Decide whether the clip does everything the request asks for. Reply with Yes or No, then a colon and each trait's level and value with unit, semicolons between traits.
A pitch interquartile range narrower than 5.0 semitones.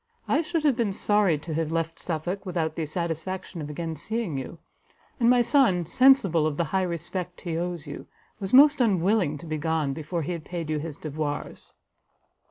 Yes: average, 4.0 semitones